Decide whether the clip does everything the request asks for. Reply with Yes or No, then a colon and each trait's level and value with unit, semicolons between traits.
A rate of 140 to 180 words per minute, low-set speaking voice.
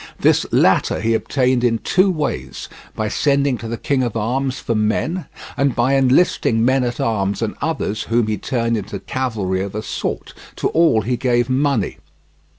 Yes: average, 175 wpm; low, 120 Hz